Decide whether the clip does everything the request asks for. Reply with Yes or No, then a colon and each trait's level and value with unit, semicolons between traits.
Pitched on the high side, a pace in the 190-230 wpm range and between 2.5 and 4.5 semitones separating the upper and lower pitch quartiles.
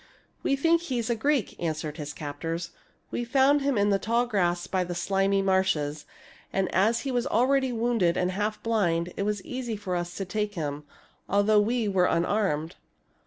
No: high, 200 Hz; average, 195 wpm; average, 5.1 semitones